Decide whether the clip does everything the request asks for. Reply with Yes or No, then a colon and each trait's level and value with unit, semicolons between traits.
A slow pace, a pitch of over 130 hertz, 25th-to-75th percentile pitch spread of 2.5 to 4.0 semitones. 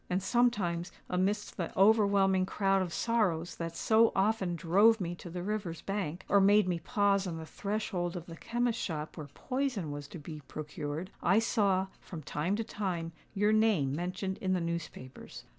No: average, 175 wpm; medium, 185 Hz; average, 3.7 semitones